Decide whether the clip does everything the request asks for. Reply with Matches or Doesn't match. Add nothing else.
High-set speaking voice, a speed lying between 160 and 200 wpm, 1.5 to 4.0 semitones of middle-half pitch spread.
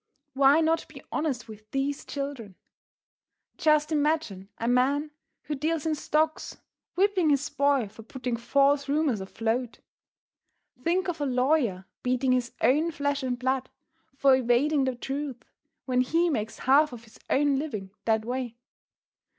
Doesn't match